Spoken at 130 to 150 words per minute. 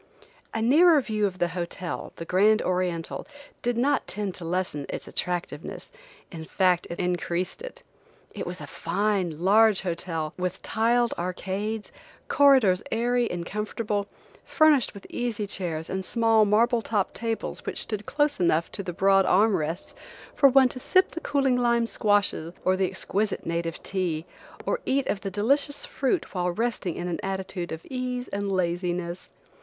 No: average, 160 wpm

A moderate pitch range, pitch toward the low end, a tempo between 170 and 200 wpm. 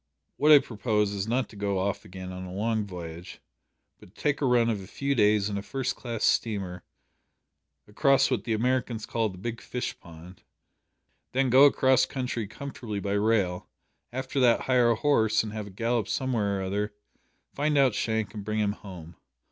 Yes: average, 4.1 semitones; low, 110 Hz; average, 190 wpm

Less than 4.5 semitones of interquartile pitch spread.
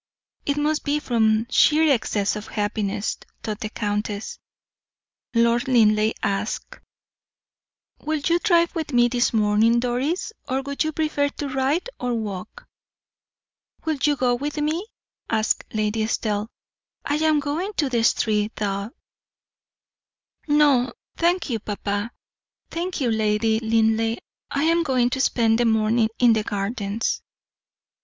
No: average, 5.3 semitones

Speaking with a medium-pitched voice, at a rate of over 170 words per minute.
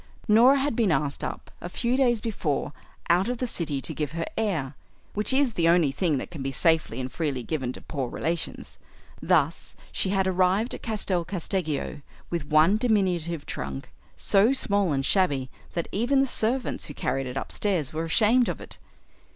Yes: medium, 175 Hz; average, 185 wpm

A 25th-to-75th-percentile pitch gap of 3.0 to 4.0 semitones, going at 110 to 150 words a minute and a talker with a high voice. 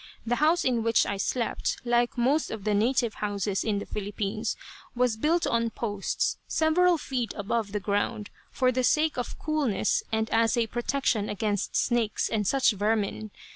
No: average, 3.5 semitones; average, 170 wpm; high, 230 Hz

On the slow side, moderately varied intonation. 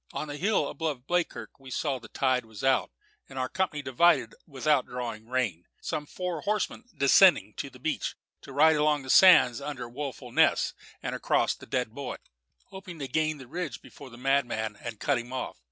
No: average, 200 wpm; average, 3.7 semitones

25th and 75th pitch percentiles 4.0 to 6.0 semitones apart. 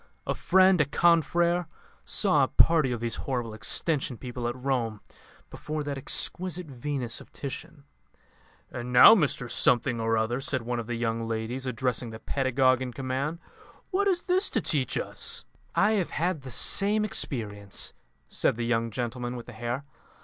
Yes: average, 4.8 semitones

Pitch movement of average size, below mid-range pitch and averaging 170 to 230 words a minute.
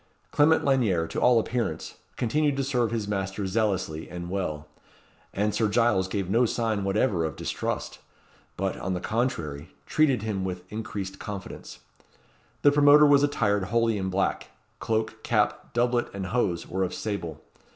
No: average, 4.2 semitones; low, 105 Hz; average, 155 wpm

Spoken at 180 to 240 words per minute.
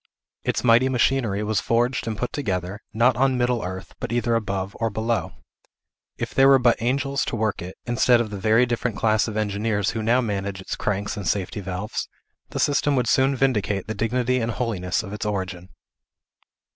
Yes: average, 190 wpm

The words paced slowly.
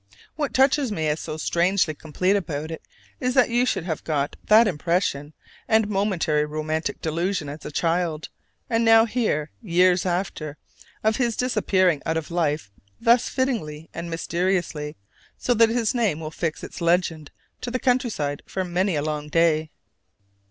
No: average, 160 wpm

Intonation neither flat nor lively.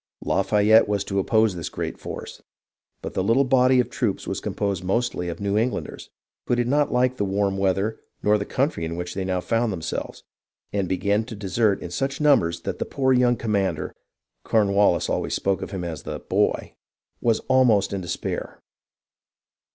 Yes: average, 4.2 semitones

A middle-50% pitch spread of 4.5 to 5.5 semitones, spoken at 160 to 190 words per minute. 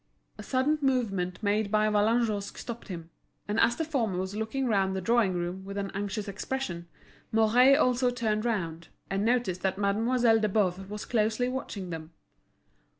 No: average, 3.8 semitones; average, 165 wpm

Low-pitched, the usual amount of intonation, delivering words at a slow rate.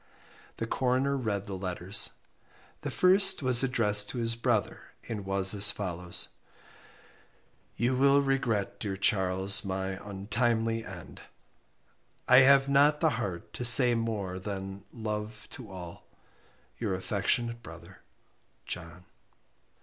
Yes: low, 105 Hz; average, 4.5 semitones; slow, 120 wpm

